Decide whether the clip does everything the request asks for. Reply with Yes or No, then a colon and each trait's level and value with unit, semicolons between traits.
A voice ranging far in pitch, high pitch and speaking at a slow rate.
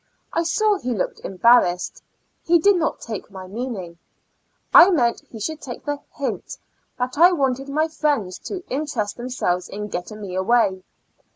No: wide, 7.4 semitones; high, 245 Hz; average, 160 wpm